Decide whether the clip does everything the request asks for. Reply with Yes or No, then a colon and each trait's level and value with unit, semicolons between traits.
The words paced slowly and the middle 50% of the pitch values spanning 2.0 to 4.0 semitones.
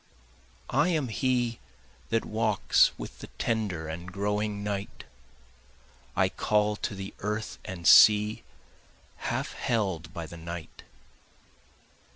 Yes: slow, 115 wpm; average, 3.5 semitones